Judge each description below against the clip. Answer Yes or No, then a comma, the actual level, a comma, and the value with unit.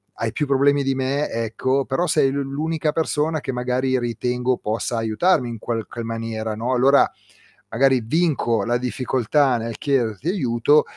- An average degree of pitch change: Yes, average, 3.4 semitones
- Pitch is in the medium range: No, low, 130 Hz